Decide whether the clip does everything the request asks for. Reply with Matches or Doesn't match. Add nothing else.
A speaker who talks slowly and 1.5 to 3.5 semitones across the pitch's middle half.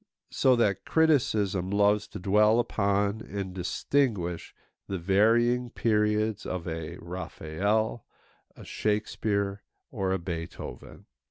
Matches